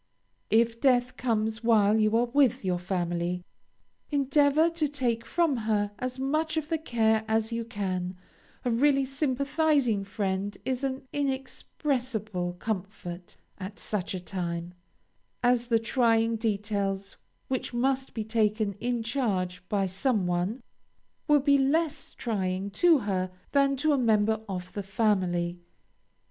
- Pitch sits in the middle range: No, high, 225 Hz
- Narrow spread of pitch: No, average, 5.2 semitones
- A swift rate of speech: No, slow, 135 wpm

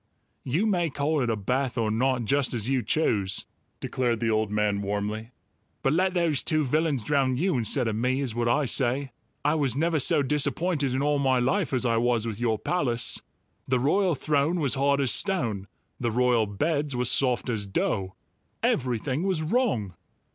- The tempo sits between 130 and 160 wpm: No, average, 185 wpm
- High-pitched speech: No, low, 130 Hz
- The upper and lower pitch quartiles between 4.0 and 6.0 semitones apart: Yes, average, 4.3 semitones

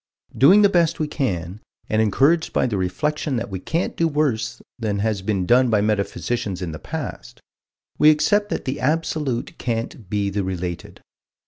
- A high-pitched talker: No, low, 115 Hz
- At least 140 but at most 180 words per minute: Yes, average, 175 wpm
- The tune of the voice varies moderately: No, wide, 7.2 semitones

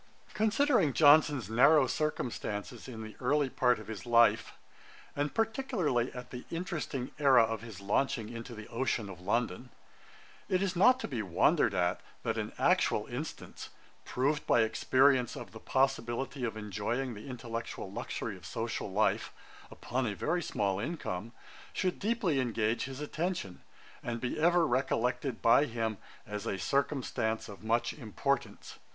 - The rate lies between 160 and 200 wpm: No, average, 150 wpm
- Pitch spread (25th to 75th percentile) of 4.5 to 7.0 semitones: Yes, average, 4.8 semitones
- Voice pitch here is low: Yes, low, 125 Hz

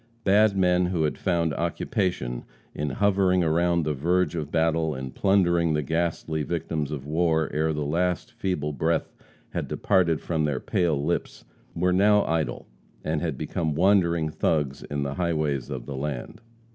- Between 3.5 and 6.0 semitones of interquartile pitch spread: No, average, 3.0 semitones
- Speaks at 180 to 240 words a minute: No, average, 160 wpm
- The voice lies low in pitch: Yes, very low, 80 Hz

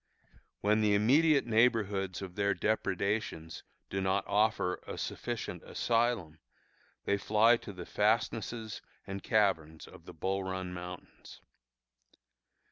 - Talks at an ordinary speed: No, slow, 120 wpm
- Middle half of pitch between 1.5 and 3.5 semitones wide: Yes, average, 2.9 semitones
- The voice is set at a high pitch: No, low, 100 Hz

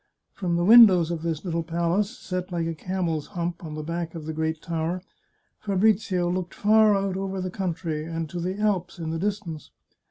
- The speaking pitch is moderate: Yes, medium, 175 Hz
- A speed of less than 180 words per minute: No, average, 195 wpm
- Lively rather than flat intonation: No, average, 2.8 semitones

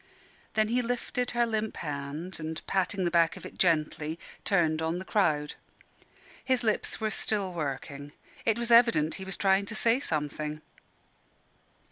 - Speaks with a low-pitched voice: No, medium, 185 Hz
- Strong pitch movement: Yes, wide, 6.0 semitones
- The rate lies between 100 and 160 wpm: Yes, average, 155 wpm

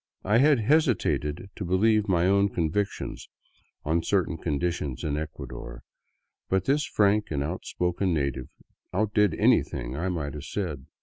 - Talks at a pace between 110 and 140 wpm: Yes, slow, 135 wpm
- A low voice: Yes, very low, 90 Hz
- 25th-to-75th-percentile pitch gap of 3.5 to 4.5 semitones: No, wide, 5.5 semitones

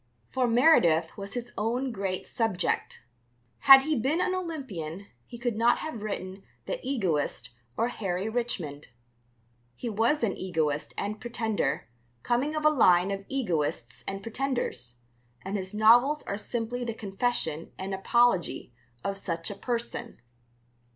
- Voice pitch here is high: Yes, high, 215 Hz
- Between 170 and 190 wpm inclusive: No, average, 140 wpm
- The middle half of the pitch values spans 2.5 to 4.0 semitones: No, average, 4.8 semitones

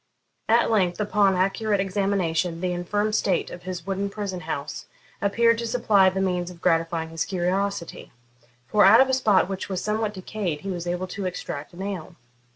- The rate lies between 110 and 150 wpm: No, average, 180 wpm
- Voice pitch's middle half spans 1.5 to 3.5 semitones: Yes, average, 2.7 semitones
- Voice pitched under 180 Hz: No, high, 190 Hz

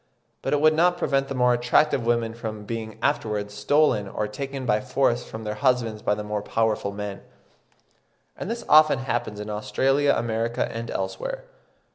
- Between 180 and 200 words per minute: No, average, 170 wpm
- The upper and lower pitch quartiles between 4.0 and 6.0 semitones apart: Yes, average, 4.4 semitones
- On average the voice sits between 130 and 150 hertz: No, low, 115 Hz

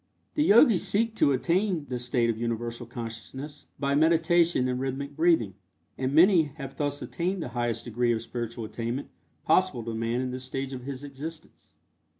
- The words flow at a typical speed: Yes, average, 170 wpm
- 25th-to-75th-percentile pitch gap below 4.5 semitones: No, average, 5.3 semitones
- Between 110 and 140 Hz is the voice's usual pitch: Yes, low, 135 Hz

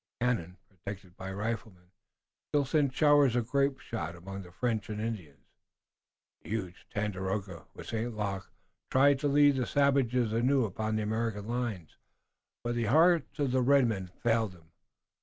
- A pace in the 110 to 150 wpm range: No, average, 165 wpm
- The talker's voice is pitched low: Yes, low, 115 Hz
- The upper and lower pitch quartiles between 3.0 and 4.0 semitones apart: No, average, 5.0 semitones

